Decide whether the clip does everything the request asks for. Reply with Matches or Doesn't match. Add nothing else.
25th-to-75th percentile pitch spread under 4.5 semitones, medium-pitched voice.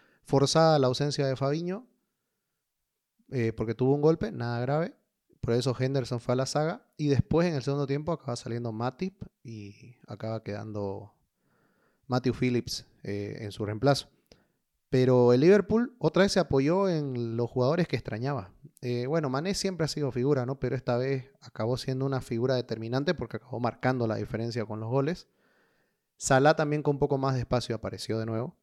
Doesn't match